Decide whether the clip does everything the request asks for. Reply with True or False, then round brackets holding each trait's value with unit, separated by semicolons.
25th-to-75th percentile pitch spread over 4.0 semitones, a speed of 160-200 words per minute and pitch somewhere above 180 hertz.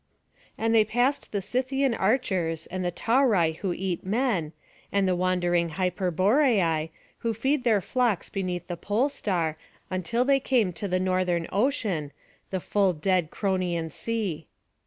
False (4.6 semitones; 145 wpm; 190 Hz)